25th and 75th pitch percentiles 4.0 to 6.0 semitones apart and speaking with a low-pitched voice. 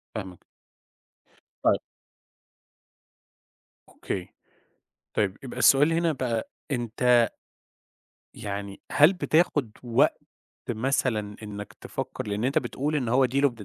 Yes: average, 4.6 semitones; low, 120 Hz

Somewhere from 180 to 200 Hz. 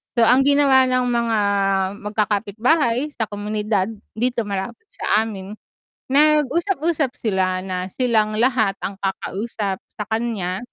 No: high, 225 Hz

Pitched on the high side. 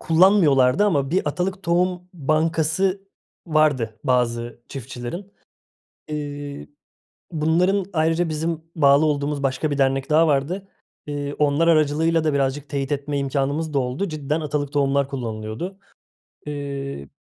No: medium, 150 Hz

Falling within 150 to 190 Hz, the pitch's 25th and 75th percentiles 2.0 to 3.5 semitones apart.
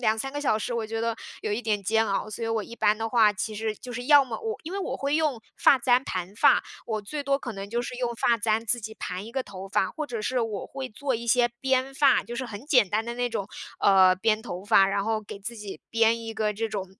No: high, 225 Hz; average, 2.9 semitones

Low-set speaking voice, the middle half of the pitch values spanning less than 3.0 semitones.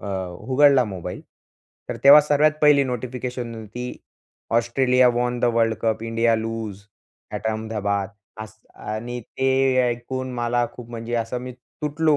Yes: low, 120 Hz; narrow, 2.4 semitones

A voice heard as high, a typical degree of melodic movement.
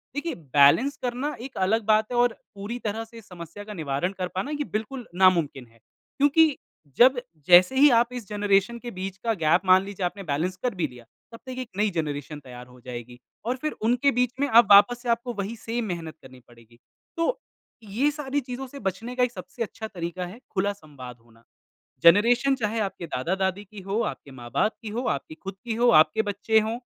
No: high, 205 Hz; wide, 6.0 semitones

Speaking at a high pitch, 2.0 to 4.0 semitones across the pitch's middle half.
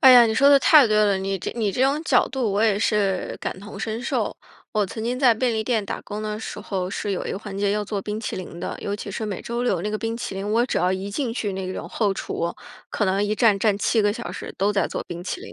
Yes: high, 210 Hz; average, 2.8 semitones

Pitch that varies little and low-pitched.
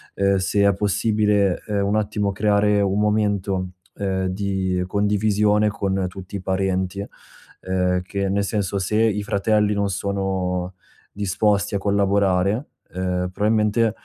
Yes: narrow, 1.6 semitones; low, 100 Hz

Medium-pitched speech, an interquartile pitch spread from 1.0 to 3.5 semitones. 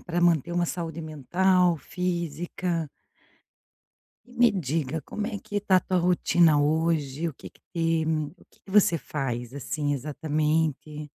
Yes: medium, 165 Hz; average, 3.0 semitones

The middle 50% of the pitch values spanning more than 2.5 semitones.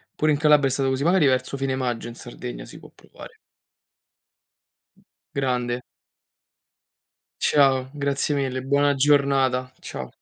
No: narrow, 1.9 semitones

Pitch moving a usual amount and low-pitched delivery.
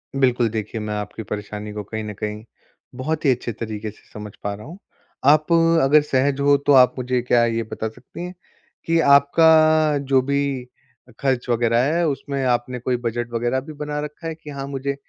Yes: average, 4.3 semitones; low, 130 Hz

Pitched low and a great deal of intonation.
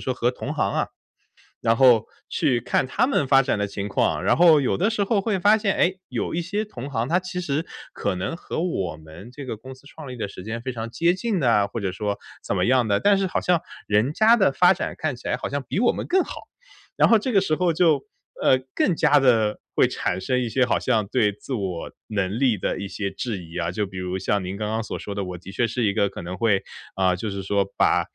Yes: low, 125 Hz; wide, 8.6 semitones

